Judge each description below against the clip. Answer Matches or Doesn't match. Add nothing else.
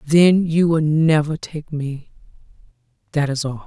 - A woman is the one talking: Matches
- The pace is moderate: Matches